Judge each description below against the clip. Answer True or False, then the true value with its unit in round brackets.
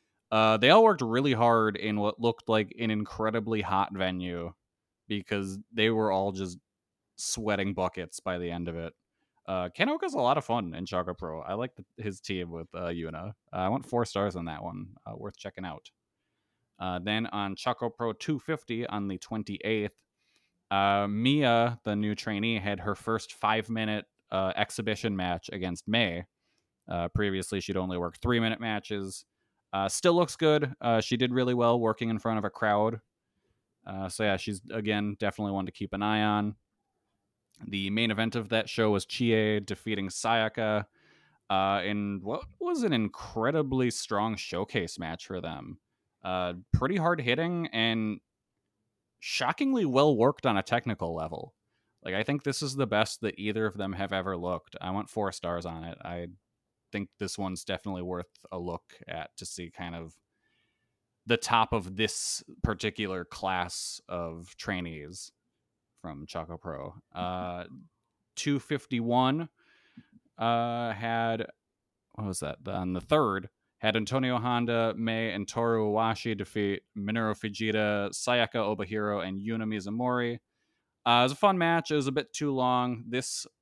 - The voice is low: True (105 Hz)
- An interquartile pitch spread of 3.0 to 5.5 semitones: True (3.4 semitones)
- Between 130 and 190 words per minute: True (165 wpm)